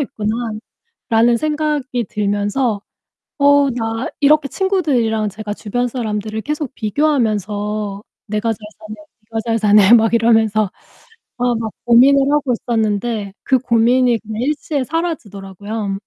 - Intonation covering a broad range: No, average, 4.0 semitones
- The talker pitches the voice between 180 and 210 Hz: No, high, 230 Hz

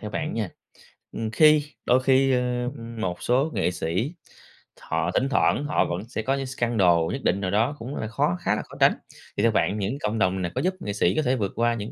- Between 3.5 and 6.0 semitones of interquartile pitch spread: Yes, average, 4.7 semitones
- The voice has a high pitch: No, low, 115 Hz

